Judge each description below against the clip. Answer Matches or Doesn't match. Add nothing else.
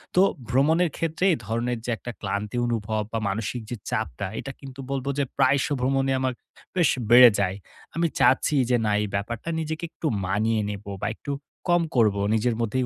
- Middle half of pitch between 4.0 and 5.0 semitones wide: Matches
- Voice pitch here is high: Doesn't match